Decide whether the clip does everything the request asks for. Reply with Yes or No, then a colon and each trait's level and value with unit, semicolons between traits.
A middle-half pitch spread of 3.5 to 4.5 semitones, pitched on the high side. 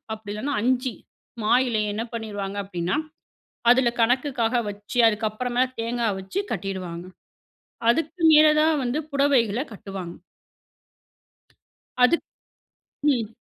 Yes: average, 3.9 semitones; high, 230 Hz